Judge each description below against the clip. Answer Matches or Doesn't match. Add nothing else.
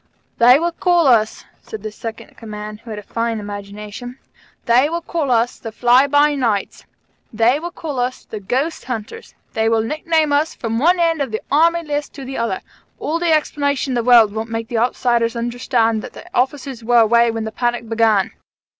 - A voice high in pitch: Matches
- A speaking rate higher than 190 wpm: Matches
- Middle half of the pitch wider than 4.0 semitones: Matches